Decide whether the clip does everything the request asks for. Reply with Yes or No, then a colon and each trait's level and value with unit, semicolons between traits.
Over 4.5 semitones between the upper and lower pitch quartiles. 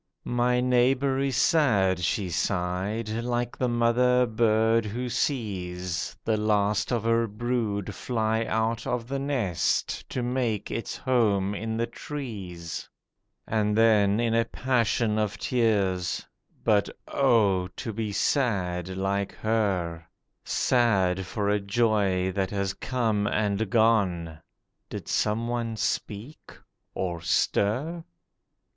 No: average, 3.4 semitones